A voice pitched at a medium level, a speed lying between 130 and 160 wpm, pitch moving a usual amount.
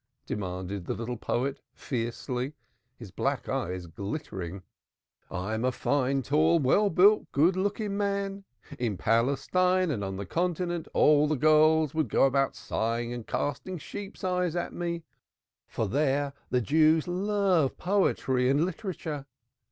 No: medium, 145 Hz; average, 140 wpm; wide, 6.9 semitones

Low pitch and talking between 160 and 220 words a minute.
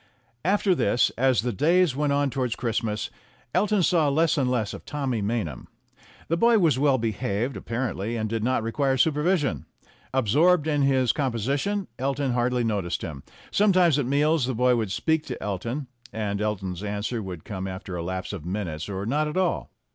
Yes: low, 125 Hz; average, 175 wpm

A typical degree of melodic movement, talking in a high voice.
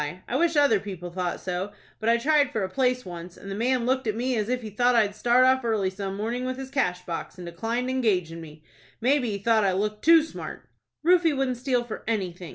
Yes: average, 5.0 semitones; high, 225 Hz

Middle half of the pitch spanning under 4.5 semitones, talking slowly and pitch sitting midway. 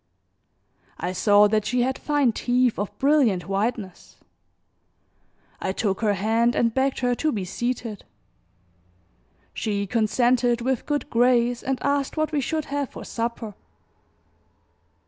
No: average, 3.8 semitones; slow, 130 wpm; high, 240 Hz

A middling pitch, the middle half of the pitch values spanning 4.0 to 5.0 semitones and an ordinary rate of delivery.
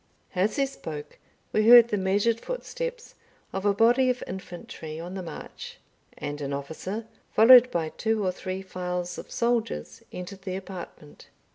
No: high, 195 Hz; average, 4.6 semitones; average, 155 wpm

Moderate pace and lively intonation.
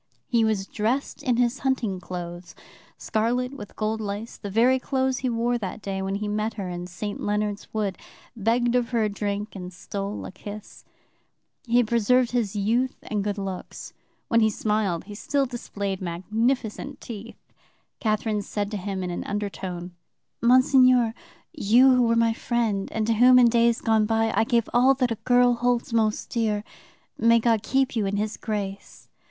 No: average, 180 wpm; average, 2.9 semitones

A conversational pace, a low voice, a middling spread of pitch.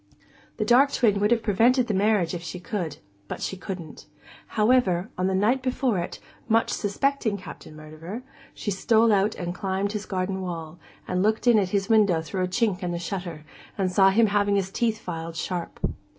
No: average, 195 wpm; high, 195 Hz; average, 3.5 semitones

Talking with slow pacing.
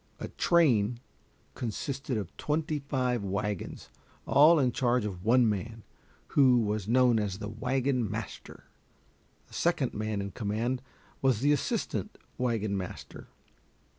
Yes: slow, 130 wpm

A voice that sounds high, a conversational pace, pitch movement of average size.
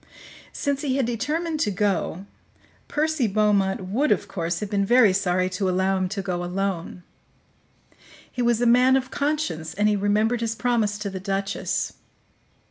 Yes: high, 210 Hz; average, 165 wpm; average, 4.4 semitones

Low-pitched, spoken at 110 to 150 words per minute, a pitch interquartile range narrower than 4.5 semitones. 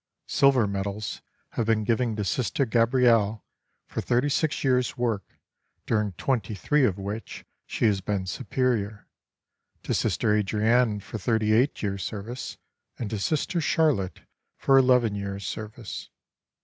Yes: low, 110 Hz; slow, 135 wpm; average, 3.6 semitones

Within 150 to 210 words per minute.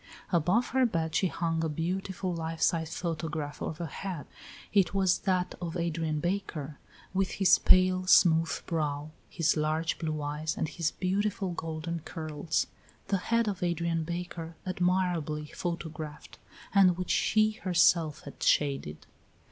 No: average, 140 wpm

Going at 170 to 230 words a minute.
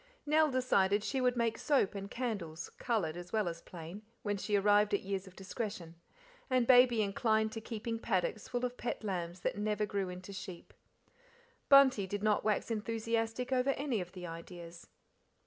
Yes: average, 175 wpm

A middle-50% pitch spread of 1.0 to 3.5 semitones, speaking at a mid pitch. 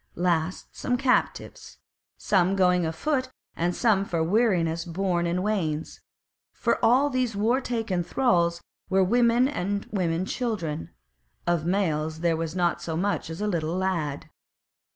No: average, 4.6 semitones; medium, 180 Hz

